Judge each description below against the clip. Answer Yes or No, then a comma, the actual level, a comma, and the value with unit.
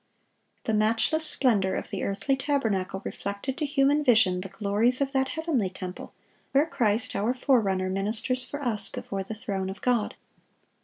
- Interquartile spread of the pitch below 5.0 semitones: No, average, 5.3 semitones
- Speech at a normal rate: Yes, average, 160 wpm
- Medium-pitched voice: No, high, 225 Hz